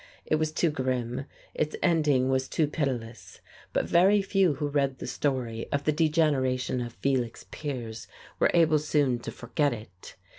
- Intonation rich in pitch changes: No, average, 3.7 semitones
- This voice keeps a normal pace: Yes, average, 160 wpm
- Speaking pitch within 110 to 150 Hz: Yes, medium, 140 Hz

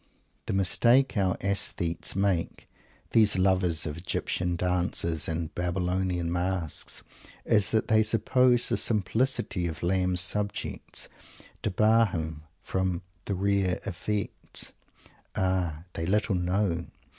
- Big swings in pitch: No, average, 2.9 semitones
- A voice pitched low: Yes, very low, 95 Hz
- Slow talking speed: Yes, slow, 110 wpm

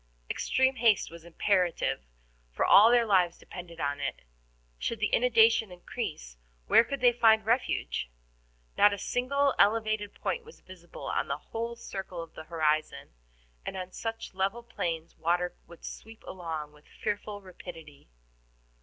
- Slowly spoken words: No, average, 145 wpm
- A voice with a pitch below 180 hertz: No, high, 195 Hz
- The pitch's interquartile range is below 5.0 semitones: No, average, 5.3 semitones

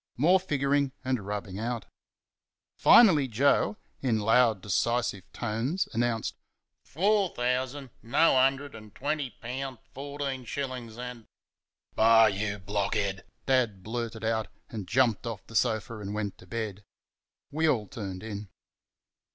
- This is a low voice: Yes, low, 115 Hz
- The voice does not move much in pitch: No, average, 4.0 semitones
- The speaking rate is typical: No, slow, 130 wpm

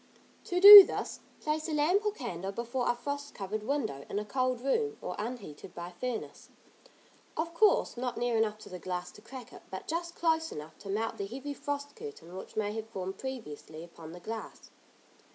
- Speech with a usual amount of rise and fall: No, wide, 6.9 semitones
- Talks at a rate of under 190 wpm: No, average, 195 wpm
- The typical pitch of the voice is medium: No, high, 240 Hz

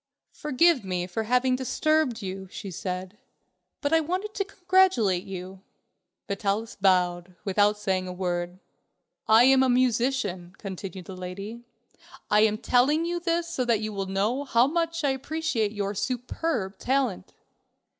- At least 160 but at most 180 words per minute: No, average, 145 wpm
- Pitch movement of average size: No, wide, 6.2 semitones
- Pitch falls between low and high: No, high, 220 Hz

